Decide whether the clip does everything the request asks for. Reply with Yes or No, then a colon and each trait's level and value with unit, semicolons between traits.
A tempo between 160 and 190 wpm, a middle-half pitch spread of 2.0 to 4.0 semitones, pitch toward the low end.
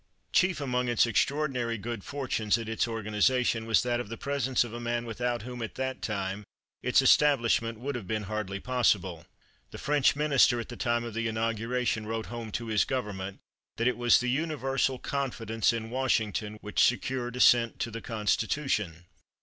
Yes: average, 175 wpm; narrow, 2.5 semitones; low, 120 Hz